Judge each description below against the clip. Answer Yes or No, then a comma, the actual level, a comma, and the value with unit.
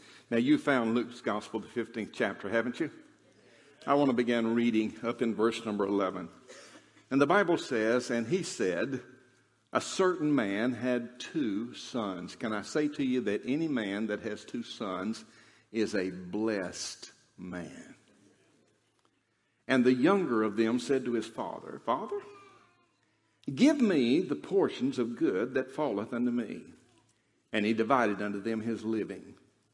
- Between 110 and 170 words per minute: Yes, average, 155 wpm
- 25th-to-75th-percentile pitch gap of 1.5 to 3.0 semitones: No, average, 3.9 semitones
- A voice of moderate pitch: No, low, 120 Hz